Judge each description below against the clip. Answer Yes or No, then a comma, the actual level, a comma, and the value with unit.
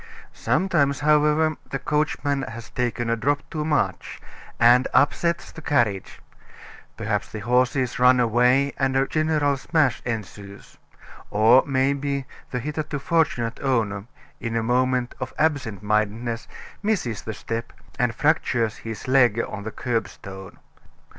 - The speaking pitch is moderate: No, low, 125 Hz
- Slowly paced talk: Yes, slow, 130 wpm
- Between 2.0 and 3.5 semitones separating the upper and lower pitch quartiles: No, average, 3.9 semitones